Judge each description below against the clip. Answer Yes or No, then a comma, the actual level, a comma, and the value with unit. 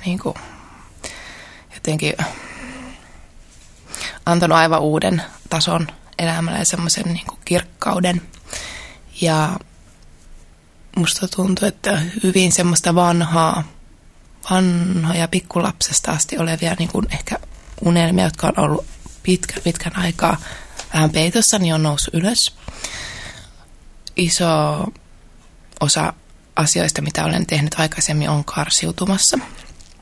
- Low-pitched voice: No, medium, 170 Hz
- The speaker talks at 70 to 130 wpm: Yes, slow, 95 wpm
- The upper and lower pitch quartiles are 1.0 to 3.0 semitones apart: Yes, narrow, 2.4 semitones